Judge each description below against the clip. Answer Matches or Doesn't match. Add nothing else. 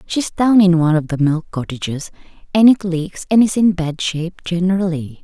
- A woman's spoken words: Matches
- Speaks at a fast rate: Doesn't match